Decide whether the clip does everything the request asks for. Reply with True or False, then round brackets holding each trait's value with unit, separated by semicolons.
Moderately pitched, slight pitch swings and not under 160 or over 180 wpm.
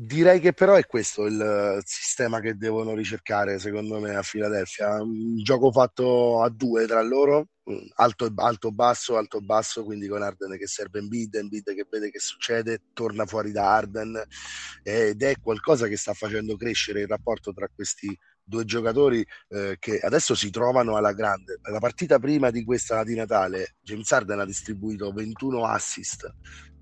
False (110 Hz; 2.1 semitones; 165 wpm)